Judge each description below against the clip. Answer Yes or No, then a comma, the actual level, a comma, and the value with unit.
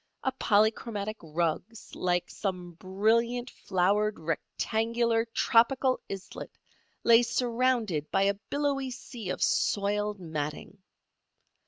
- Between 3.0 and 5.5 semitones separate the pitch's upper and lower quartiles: Yes, average, 4.1 semitones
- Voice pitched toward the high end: Yes, high, 210 Hz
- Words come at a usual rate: No, slow, 100 wpm